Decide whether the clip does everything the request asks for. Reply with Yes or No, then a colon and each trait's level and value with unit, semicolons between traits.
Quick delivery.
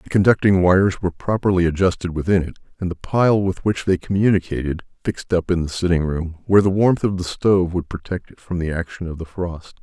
Yes: fast, 220 wpm